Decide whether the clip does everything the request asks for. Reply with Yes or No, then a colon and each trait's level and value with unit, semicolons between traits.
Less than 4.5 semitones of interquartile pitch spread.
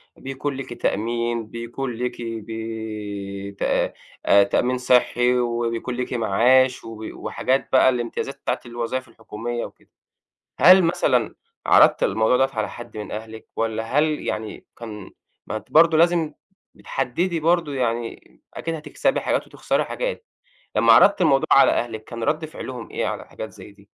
Yes: average, 3.3 semitones